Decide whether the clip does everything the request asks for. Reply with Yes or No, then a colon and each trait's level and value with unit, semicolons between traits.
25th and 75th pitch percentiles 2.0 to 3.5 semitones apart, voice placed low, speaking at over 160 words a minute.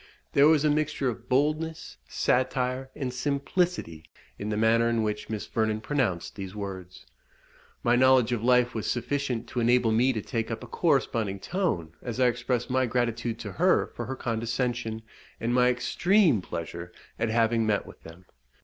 Yes: average, 3.0 semitones; low, 120 Hz; average, 170 wpm